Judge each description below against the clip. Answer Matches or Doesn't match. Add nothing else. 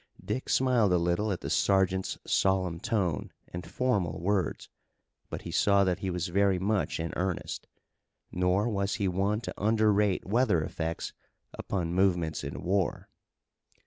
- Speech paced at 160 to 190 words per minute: Doesn't match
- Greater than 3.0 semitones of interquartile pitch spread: Doesn't match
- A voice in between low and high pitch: Doesn't match